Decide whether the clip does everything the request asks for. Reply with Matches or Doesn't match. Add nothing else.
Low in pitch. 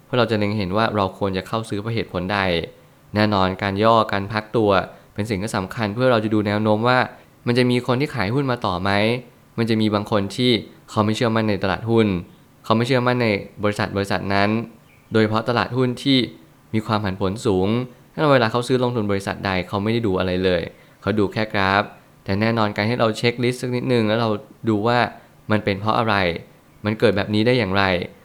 Matches